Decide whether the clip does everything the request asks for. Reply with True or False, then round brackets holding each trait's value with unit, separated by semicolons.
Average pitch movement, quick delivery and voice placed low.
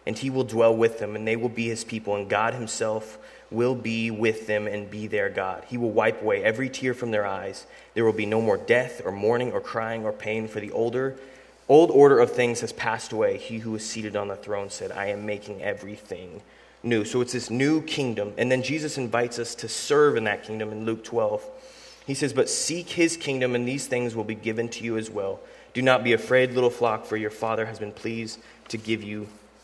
True (3.0 semitones; 235 wpm; 115 Hz)